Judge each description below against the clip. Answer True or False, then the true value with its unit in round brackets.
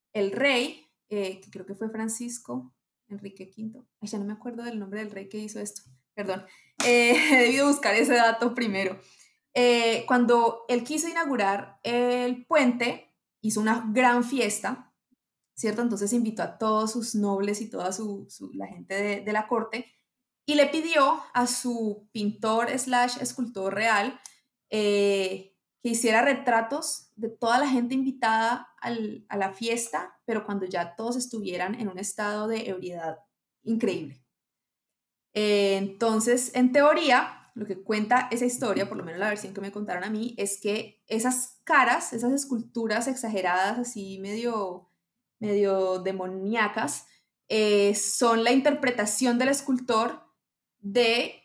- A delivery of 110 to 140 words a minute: False (150 wpm)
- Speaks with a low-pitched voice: False (225 Hz)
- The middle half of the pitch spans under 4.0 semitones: True (3.3 semitones)